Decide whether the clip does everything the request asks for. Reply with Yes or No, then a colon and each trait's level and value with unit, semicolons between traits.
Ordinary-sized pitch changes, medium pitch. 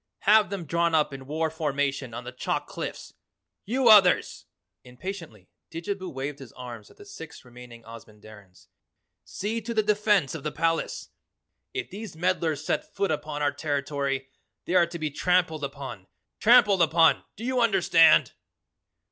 No: wide, 6.0 semitones; medium, 160 Hz